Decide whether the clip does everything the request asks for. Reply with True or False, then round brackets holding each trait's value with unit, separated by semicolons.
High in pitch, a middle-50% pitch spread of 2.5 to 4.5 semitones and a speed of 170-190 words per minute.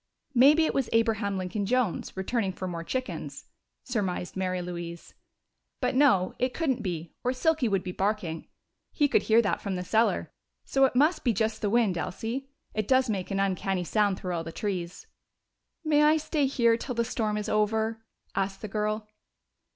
False (215 Hz; 4.9 semitones; 180 wpm)